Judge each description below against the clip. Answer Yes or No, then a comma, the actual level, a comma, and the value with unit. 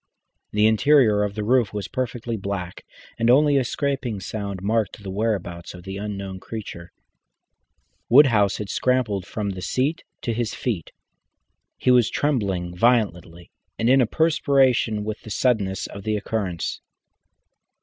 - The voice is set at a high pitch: No, low, 110 Hz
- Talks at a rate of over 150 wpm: No, average, 145 wpm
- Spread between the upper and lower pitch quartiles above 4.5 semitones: No, average, 4.1 semitones